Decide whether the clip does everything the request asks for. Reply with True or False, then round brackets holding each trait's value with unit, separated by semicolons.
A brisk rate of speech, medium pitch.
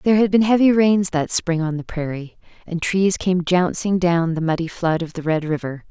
True (225 wpm; 175 Hz)